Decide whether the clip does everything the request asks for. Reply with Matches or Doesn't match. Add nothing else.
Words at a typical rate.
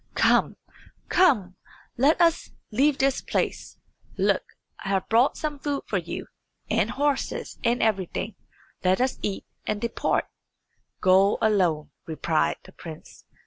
Doesn't match